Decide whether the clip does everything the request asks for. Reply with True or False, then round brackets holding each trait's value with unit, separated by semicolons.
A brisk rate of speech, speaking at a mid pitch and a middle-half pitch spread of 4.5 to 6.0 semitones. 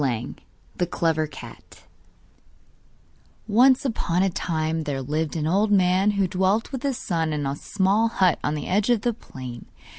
False (170 wpm; 180 Hz; 5.1 semitones)